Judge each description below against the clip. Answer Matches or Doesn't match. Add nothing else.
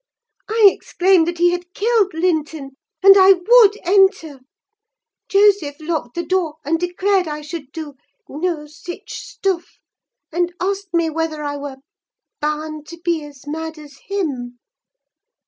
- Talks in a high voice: Matches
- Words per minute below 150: Matches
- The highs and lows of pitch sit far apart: Doesn't match